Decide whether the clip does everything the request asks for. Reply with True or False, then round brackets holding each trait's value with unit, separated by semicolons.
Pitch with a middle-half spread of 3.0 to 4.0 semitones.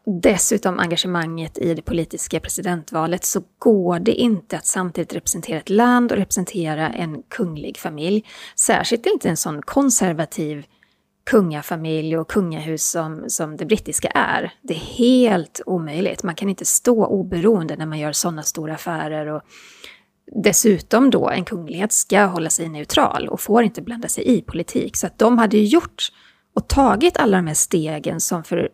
False (4.7 semitones)